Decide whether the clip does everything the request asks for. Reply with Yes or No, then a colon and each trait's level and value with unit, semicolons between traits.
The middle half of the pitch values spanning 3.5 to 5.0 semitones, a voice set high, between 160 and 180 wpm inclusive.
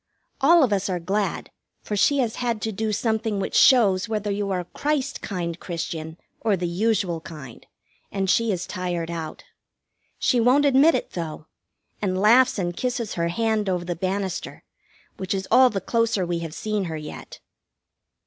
Yes: average, 4.6 semitones; high, 195 Hz; average, 175 wpm